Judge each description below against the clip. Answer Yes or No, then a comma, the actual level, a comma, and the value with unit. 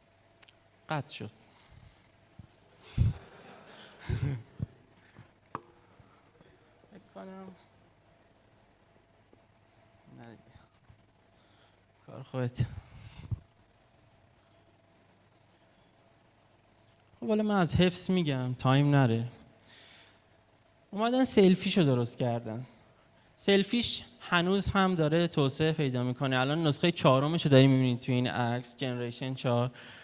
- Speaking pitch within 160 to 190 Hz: No, low, 115 Hz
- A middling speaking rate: No, slow, 70 wpm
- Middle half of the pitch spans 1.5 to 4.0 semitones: Yes, average, 3.7 semitones